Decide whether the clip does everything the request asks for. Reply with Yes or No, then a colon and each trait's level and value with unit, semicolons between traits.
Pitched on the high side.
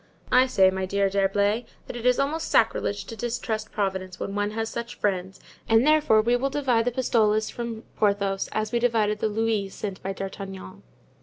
Yes: high, 215 Hz